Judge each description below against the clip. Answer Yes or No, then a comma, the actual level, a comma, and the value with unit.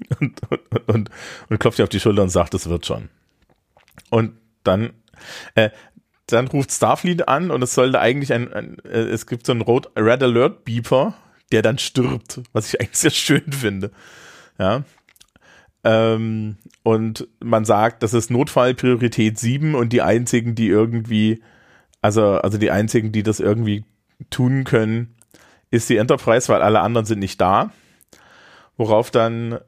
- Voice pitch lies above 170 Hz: No, low, 115 Hz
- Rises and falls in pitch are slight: Yes, narrow, 2.3 semitones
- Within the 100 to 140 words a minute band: No, average, 160 wpm